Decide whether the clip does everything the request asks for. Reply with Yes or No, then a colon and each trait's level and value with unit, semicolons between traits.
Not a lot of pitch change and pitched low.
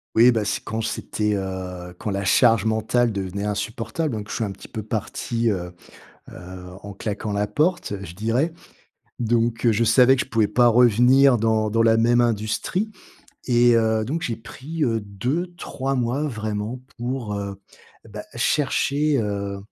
No: average, 3.1 semitones; low, 115 Hz